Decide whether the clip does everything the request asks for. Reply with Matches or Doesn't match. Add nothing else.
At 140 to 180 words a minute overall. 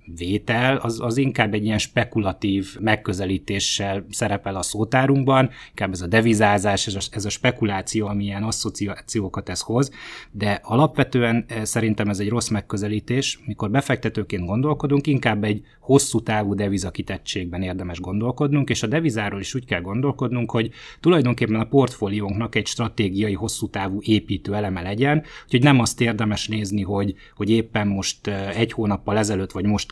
Matches